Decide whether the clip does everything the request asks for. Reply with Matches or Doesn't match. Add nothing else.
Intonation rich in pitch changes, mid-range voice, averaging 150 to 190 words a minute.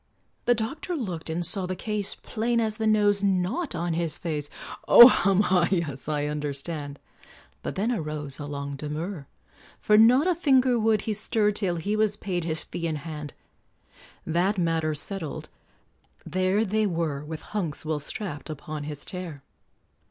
Matches